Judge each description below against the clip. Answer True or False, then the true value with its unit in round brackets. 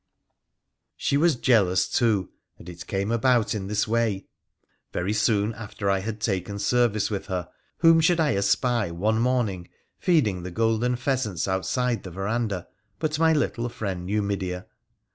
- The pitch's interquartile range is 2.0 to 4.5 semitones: True (4.1 semitones)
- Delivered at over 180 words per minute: False (150 wpm)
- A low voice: True (105 Hz)